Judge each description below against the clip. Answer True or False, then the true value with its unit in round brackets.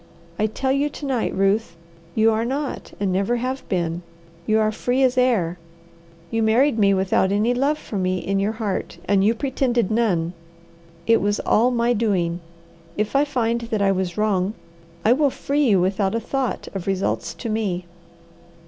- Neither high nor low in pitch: False (220 Hz)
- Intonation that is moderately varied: True (4.1 semitones)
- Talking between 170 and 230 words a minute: True (180 wpm)